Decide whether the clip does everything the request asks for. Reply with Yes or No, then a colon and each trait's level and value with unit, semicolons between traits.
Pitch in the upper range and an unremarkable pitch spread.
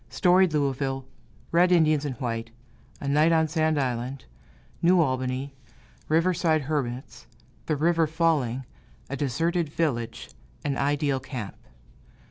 No: medium, 145 Hz; average, 3.8 semitones